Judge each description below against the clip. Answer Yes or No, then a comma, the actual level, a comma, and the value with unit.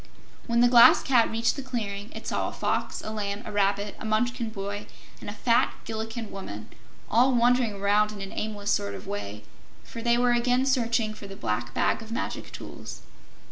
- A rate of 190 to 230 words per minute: Yes, average, 195 wpm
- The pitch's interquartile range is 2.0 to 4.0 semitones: Yes, average, 2.9 semitones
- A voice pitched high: Yes, high, 215 Hz